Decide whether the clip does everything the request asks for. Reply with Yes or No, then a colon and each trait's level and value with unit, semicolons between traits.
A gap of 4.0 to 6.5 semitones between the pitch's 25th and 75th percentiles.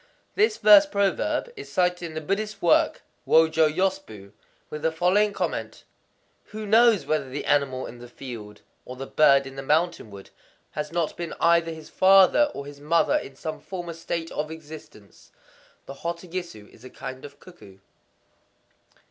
Yes: average, 5.0 semitones